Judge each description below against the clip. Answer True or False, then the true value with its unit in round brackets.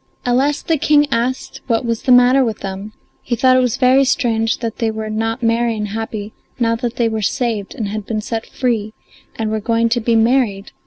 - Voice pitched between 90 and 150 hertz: False (230 Hz)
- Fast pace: True (220 wpm)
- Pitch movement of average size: False (2.3 semitones)